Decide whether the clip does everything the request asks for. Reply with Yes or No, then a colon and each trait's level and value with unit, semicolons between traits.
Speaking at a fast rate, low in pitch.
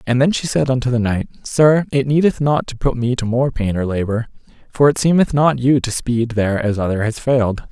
Yes: fast, 240 wpm; low, 125 Hz